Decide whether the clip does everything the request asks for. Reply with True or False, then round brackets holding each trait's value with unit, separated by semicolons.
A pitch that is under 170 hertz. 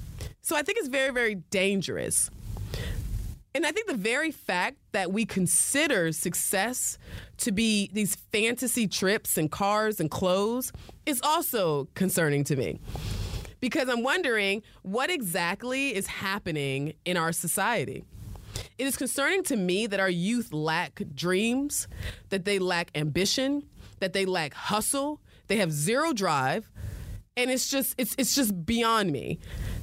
False (195 Hz)